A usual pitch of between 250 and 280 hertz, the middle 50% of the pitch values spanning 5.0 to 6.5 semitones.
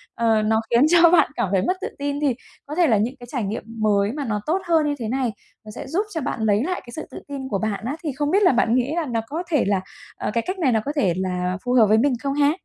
Yes: very high, 255 Hz; wide, 5.6 semitones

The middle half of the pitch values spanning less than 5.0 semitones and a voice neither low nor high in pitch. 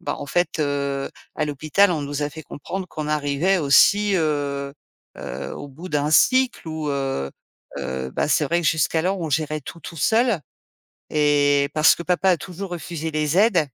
Yes: average, 3.5 semitones; medium, 155 Hz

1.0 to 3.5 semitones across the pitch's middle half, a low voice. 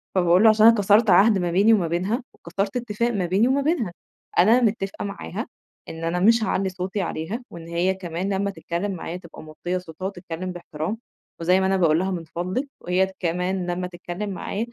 No: average, 3.1 semitones; medium, 185 Hz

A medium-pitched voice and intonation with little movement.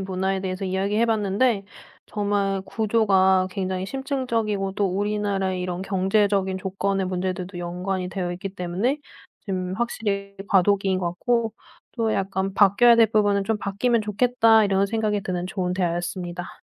No: high, 195 Hz; narrow, 2.1 semitones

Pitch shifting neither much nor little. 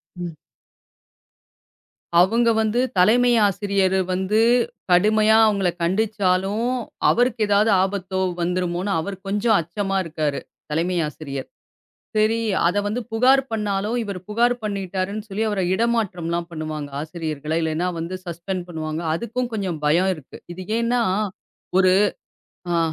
Yes: average, 3.9 semitones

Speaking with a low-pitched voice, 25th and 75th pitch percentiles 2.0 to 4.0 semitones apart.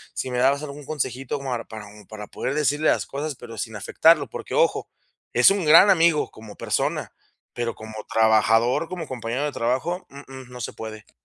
No: low, 130 Hz; average, 4.8 semitones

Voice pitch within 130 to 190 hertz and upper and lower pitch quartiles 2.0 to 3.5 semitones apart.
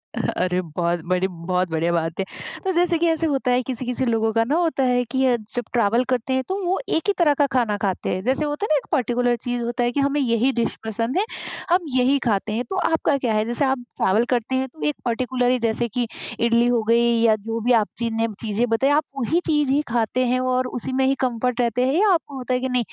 No: high, 245 Hz; average, 3.0 semitones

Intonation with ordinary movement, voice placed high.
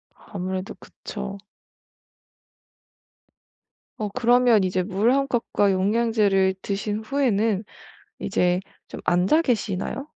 Yes: average, 3.8 semitones; high, 205 Hz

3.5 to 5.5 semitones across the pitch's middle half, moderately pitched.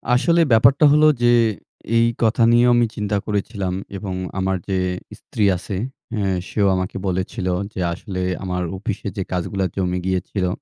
No: average, 3.8 semitones; low, 100 Hz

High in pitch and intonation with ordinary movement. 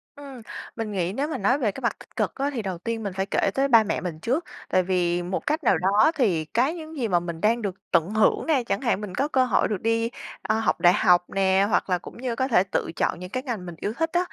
No: high, 215 Hz; wide, 5.9 semitones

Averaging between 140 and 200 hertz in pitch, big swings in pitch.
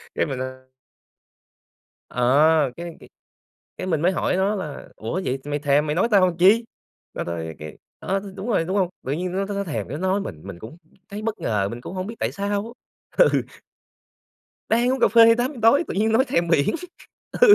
Yes: medium, 185 Hz; wide, 6.5 semitones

